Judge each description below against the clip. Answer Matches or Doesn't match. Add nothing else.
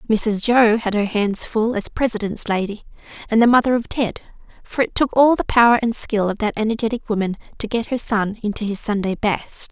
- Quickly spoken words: Matches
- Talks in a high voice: Matches